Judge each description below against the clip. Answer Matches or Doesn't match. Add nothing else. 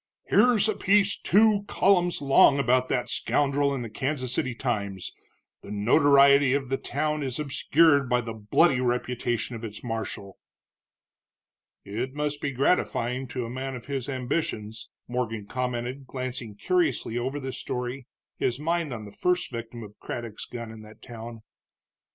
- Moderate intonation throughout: Matches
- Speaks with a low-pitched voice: Matches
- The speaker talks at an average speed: Matches